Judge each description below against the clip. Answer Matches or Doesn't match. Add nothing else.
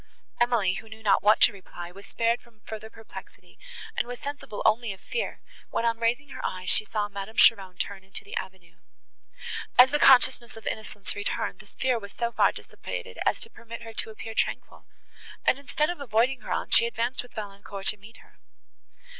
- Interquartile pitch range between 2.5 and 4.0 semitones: Matches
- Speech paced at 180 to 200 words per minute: Matches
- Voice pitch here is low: Doesn't match